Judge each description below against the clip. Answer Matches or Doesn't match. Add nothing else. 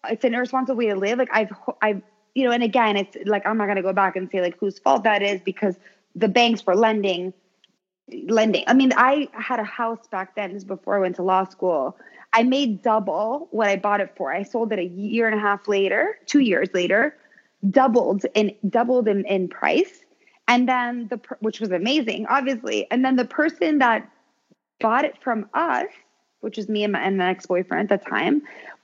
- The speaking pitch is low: Doesn't match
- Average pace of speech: Doesn't match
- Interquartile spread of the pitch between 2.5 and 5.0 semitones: Matches